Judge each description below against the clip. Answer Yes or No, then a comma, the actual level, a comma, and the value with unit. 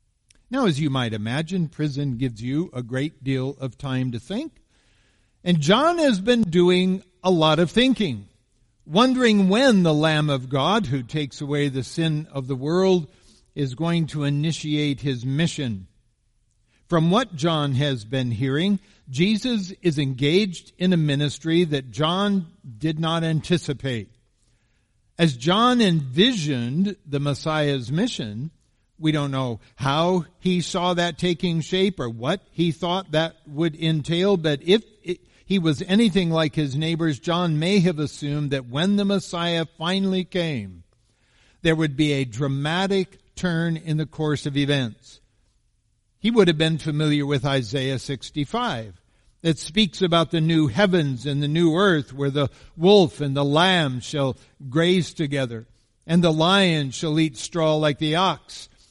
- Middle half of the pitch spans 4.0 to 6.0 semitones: Yes, average, 4.6 semitones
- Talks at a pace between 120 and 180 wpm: Yes, average, 150 wpm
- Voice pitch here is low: No, medium, 155 Hz